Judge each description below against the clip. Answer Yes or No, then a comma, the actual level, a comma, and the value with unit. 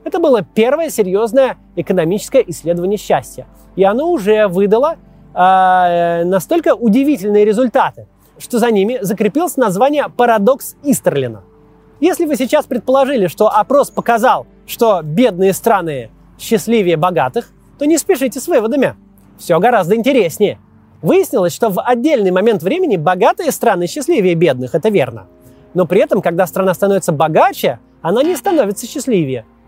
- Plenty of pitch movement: Yes, wide, 6.7 semitones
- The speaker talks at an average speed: Yes, average, 130 wpm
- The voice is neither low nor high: No, high, 215 Hz